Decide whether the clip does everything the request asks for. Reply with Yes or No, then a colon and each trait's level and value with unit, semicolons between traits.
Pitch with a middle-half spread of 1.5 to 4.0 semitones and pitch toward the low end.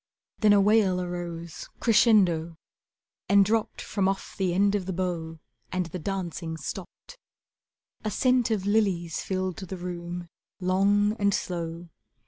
No: average, 2.8 semitones; medium, 185 Hz